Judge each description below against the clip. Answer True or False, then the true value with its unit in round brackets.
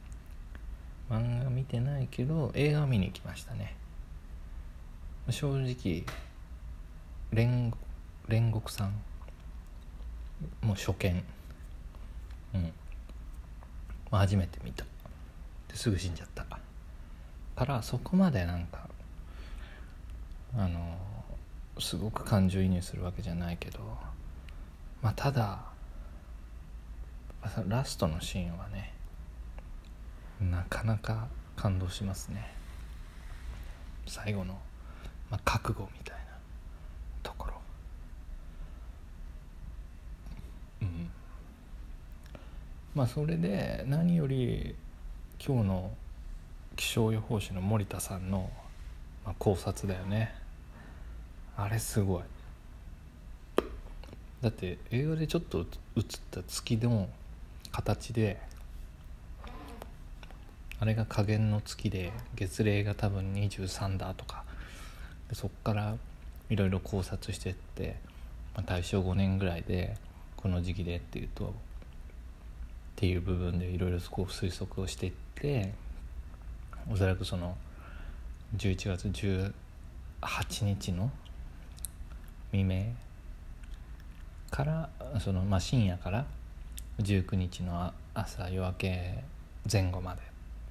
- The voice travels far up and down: False (5.0 semitones)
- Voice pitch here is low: True (85 Hz)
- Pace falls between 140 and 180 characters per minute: True (175 characters per minute)